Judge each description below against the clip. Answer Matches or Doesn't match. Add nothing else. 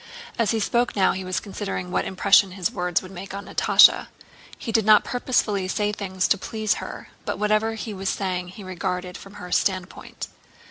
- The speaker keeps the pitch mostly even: Matches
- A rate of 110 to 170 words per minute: Doesn't match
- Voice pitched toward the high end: Matches